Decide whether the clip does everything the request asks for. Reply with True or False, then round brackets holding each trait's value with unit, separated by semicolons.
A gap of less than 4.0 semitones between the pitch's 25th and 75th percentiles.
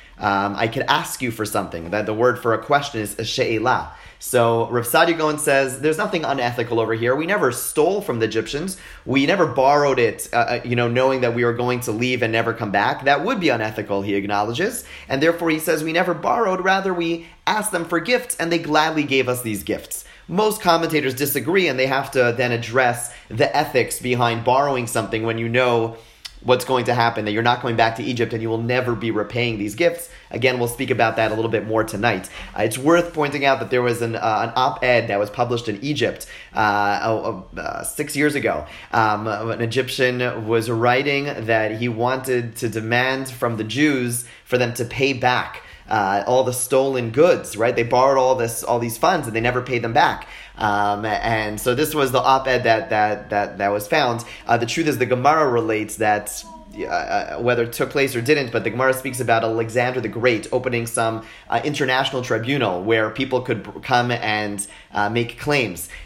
True (2.9 semitones)